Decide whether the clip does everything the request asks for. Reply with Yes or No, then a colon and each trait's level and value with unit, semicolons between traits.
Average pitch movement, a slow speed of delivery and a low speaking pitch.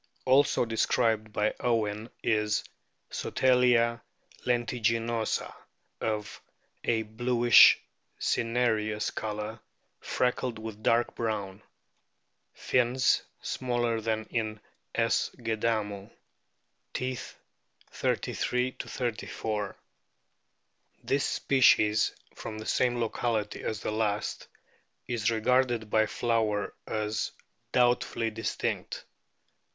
No: narrow, 2.0 semitones; slow, 85 wpm; low, 115 Hz